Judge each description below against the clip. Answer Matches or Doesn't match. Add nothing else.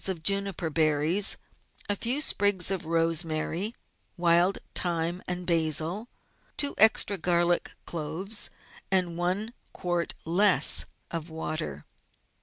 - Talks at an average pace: Doesn't match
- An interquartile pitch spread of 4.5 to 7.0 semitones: Doesn't match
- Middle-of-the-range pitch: Matches